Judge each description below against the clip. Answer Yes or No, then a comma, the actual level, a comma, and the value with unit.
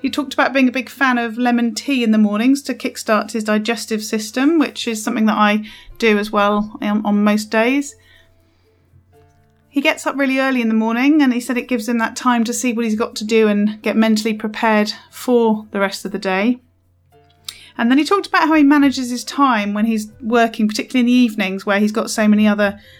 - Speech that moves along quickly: Yes, fast, 220 wpm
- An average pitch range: Yes, average, 3.2 semitones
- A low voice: No, high, 225 Hz